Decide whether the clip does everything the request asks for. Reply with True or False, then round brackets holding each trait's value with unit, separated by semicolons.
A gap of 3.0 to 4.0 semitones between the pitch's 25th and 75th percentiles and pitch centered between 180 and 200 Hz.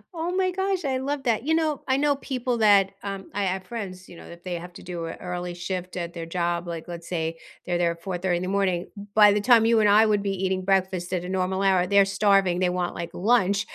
True (3.7 semitones; 190 Hz)